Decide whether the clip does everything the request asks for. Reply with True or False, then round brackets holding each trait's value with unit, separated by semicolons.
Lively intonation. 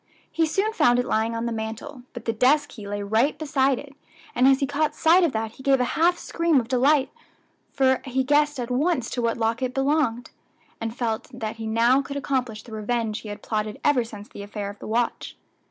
False (3.9 semitones)